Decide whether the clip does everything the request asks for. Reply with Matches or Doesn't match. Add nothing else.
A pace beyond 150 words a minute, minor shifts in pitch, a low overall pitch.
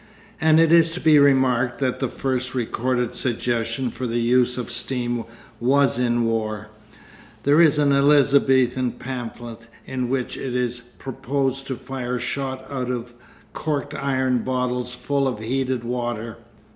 Doesn't match